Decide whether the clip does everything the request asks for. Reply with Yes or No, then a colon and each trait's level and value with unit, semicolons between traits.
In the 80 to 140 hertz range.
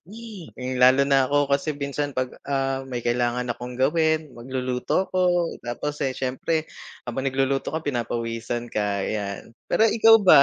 Yes: low, 135 Hz